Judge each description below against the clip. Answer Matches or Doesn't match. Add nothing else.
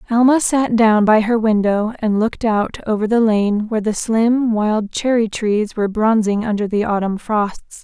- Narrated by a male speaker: Doesn't match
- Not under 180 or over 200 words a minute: Matches